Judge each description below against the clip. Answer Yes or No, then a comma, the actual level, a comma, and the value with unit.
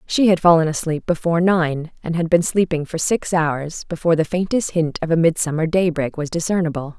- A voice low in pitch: No, medium, 165 Hz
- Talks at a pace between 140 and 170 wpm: No, average, 195 wpm